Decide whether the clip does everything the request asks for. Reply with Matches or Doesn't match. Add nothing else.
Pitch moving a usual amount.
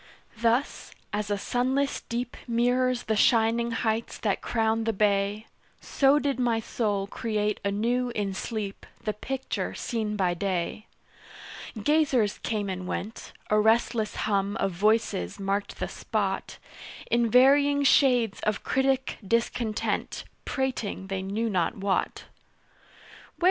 Matches